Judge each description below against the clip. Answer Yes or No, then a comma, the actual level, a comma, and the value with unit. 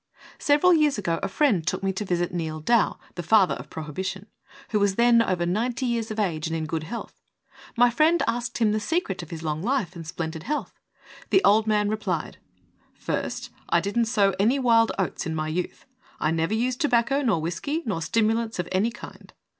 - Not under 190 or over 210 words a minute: Yes, average, 200 wpm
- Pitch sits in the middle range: No, high, 210 Hz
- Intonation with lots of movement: Yes, wide, 5.7 semitones